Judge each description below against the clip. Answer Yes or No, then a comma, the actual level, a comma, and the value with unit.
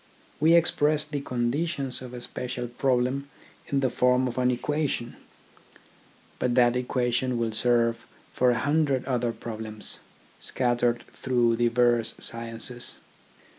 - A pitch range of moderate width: No, narrow, 2.0 semitones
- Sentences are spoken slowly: Yes, slow, 125 wpm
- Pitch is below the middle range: Yes, low, 125 Hz